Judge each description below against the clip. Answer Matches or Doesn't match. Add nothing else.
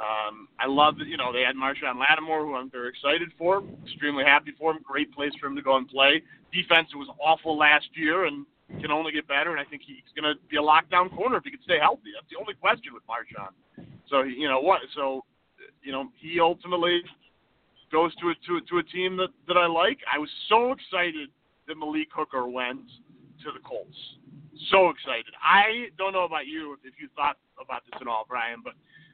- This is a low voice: Doesn't match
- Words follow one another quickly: Matches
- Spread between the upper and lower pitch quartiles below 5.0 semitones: Matches